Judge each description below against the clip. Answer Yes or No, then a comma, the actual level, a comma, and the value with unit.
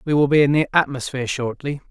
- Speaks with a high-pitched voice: No, medium, 140 Hz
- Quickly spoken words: Yes, fast, 220 wpm